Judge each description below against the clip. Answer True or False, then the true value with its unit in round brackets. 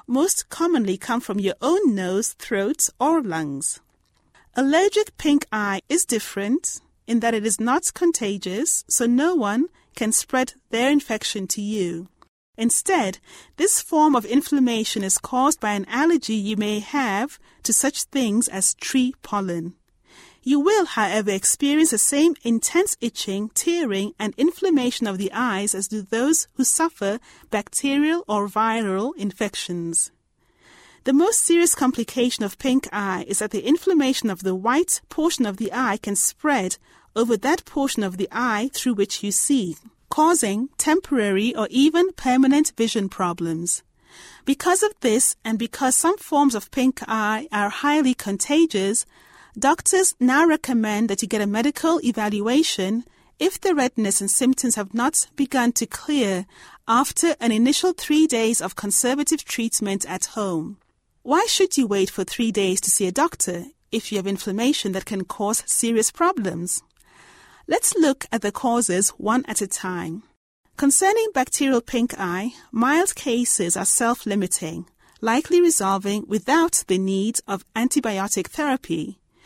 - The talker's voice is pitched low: False (235 Hz)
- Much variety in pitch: True (6.3 semitones)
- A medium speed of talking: True (150 wpm)